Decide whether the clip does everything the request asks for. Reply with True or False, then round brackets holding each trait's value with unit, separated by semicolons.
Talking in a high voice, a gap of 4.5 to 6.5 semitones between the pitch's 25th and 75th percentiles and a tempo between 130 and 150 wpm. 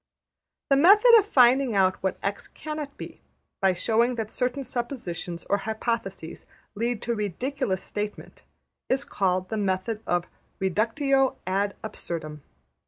True (220 Hz; 5.4 semitones; 140 wpm)